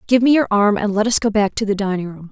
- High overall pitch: Yes, high, 210 Hz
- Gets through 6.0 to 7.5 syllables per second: Yes, 6.5 syllables/s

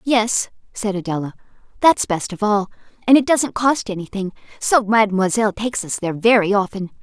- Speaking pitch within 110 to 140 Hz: No, high, 210 Hz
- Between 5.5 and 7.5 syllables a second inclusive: Yes, 5.6 syllables/s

